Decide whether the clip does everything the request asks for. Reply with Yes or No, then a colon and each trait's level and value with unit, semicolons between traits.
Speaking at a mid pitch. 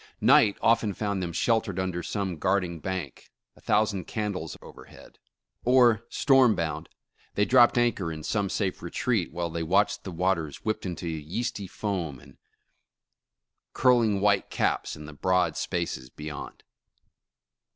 No: very low, 95 Hz